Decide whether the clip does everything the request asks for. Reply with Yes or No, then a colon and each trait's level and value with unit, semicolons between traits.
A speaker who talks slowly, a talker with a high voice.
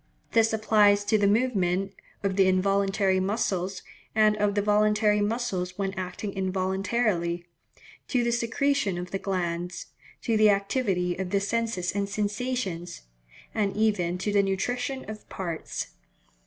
Yes: slow, 130 wpm; high, 200 Hz